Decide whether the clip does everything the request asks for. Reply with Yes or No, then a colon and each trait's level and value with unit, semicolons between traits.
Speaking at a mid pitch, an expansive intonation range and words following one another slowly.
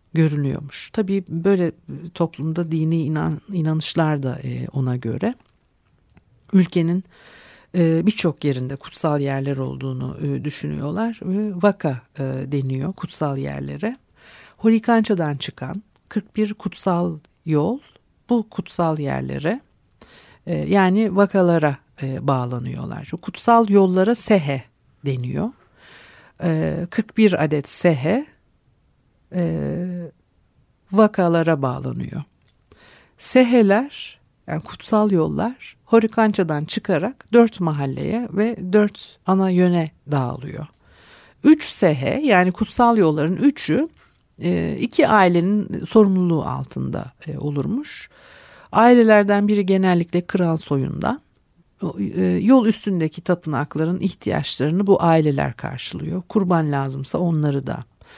Yes: medium, 175 Hz; wide, 6.0 semitones; slow, 85 wpm